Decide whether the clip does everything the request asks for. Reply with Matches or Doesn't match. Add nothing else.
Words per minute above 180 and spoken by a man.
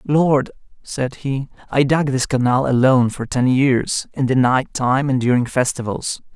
Doesn't match